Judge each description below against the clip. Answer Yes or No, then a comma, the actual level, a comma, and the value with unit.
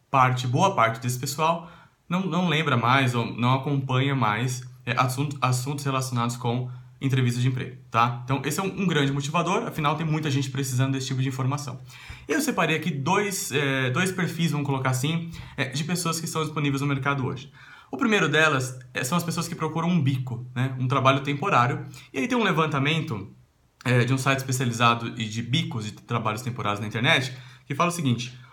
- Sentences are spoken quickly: Yes, fast, 190 wpm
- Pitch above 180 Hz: No, low, 135 Hz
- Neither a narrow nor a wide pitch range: Yes, average, 3.9 semitones